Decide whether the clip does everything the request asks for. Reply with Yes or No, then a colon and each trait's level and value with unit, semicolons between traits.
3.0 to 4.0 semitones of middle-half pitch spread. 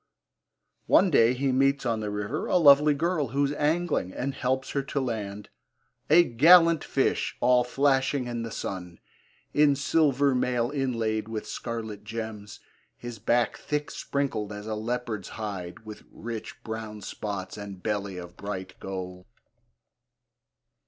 No: average, 4.9 semitones